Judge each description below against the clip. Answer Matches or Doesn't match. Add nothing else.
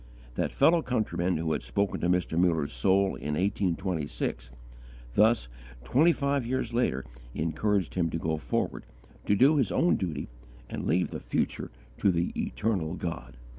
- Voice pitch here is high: Doesn't match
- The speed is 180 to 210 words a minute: Doesn't match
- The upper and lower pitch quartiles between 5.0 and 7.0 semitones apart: Matches